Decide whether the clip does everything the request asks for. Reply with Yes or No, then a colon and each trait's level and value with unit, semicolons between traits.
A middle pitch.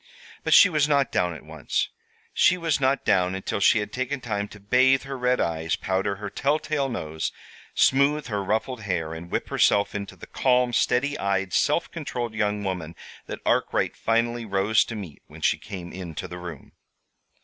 No: low, 105 Hz